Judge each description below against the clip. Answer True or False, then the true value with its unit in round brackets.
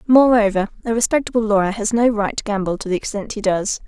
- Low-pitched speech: False (215 Hz)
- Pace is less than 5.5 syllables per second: False (6.2 syllables/s)